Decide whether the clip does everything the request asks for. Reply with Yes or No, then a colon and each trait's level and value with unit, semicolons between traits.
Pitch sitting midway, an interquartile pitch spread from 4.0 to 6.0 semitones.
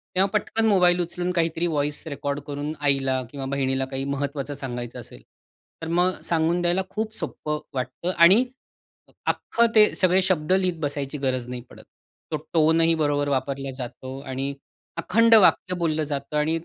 Yes: medium, 150 Hz; average, 4.3 semitones